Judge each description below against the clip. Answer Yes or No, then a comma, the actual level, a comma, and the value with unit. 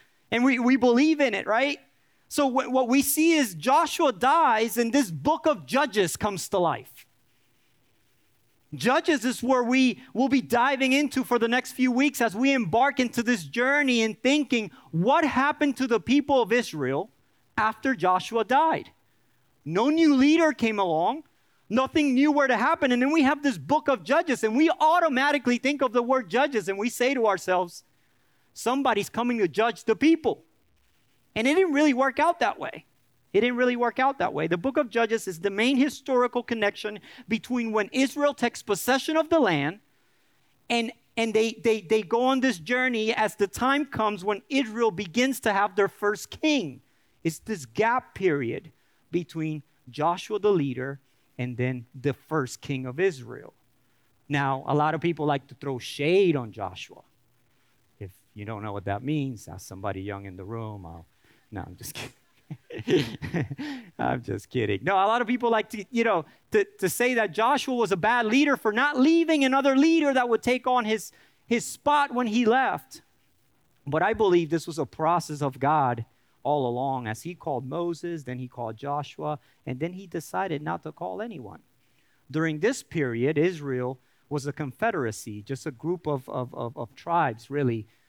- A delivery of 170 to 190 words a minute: Yes, average, 180 wpm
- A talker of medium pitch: No, high, 220 Hz